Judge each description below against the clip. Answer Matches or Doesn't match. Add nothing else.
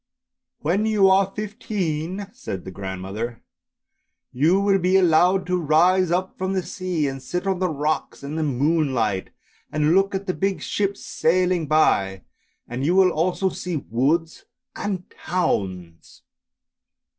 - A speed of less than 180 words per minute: Matches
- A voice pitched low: Doesn't match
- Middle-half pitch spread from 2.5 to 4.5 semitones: Doesn't match